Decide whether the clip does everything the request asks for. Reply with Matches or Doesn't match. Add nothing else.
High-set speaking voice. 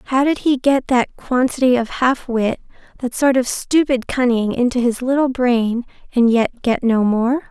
Matches